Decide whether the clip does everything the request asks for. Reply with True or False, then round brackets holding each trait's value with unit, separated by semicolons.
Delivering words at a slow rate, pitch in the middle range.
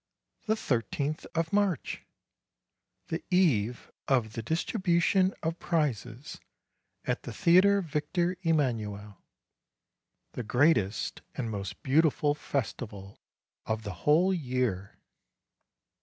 True (100 wpm; 145 Hz)